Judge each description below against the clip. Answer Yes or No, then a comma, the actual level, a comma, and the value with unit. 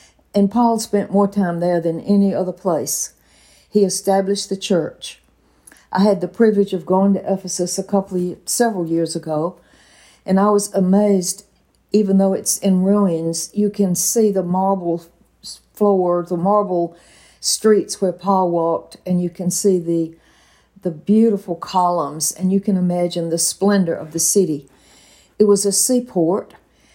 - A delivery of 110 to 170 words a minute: Yes, average, 155 wpm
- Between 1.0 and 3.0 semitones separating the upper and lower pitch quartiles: Yes, average, 2.7 semitones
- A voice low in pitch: No, high, 190 Hz